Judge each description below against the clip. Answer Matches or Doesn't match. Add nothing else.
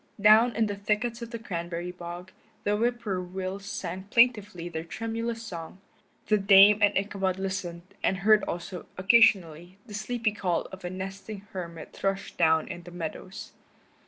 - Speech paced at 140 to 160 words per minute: Matches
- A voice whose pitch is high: Matches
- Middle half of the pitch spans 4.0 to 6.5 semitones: Doesn't match